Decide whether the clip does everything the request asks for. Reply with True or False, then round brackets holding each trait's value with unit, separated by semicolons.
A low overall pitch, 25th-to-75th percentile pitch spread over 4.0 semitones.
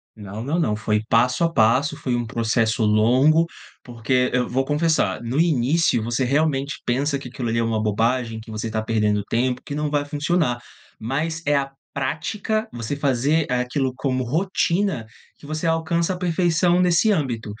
True (130 Hz; 5.3 semitones)